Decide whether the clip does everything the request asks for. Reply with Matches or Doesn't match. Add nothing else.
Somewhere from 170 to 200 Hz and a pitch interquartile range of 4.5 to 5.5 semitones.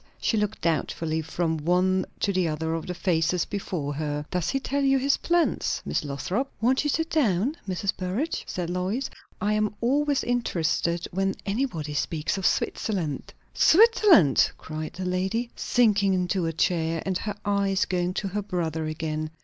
Matches